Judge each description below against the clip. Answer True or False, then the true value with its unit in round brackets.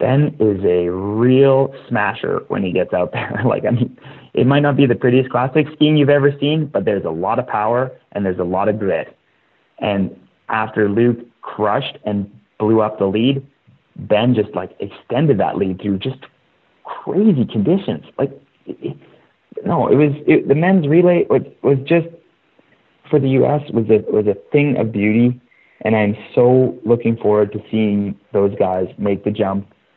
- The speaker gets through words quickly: False (180 wpm)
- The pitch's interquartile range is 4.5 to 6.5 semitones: True (4.9 semitones)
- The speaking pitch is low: True (120 Hz)